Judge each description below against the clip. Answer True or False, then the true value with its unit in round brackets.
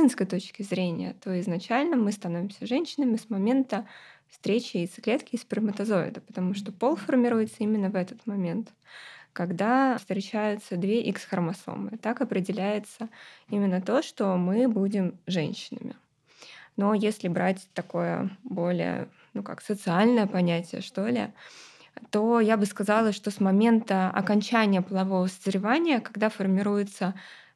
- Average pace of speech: True (120 wpm)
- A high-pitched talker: True (205 Hz)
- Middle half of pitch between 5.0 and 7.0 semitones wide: False (3.3 semitones)